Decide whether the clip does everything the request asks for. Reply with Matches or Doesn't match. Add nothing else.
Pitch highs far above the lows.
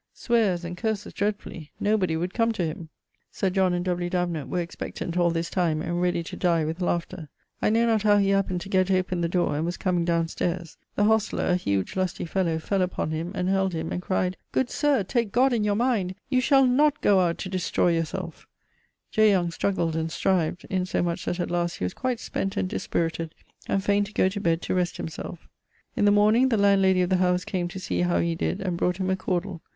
Doesn't match